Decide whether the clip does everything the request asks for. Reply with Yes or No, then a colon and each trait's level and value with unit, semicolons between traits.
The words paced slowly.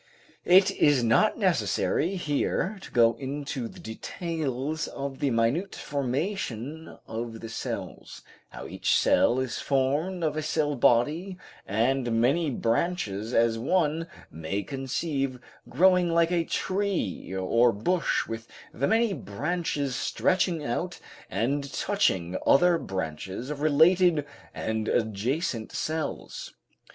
Yes: slow, 120 wpm